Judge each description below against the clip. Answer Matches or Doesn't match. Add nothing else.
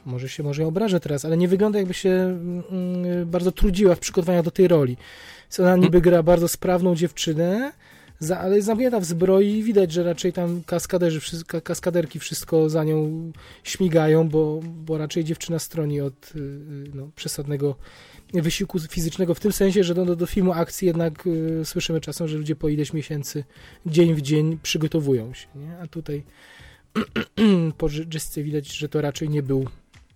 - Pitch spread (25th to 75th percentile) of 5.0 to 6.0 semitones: Doesn't match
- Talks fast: Matches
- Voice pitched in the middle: Matches